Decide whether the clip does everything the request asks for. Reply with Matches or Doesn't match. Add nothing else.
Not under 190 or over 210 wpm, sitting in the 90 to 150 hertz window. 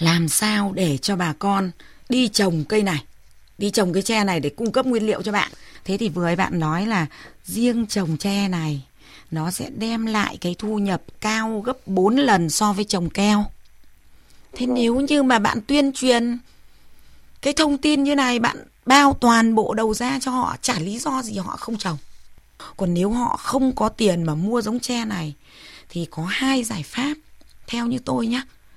Doesn't match